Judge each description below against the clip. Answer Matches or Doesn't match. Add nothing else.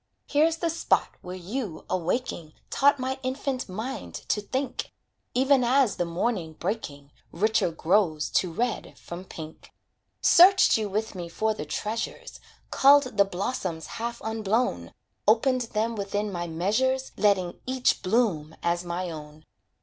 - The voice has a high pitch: Matches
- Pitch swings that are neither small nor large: Doesn't match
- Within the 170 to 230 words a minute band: Doesn't match